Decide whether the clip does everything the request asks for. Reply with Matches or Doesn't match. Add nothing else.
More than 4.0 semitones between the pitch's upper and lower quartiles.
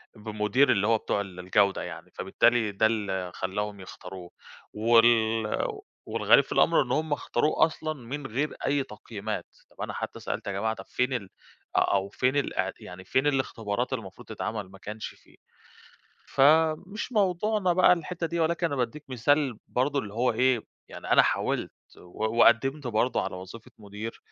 Matches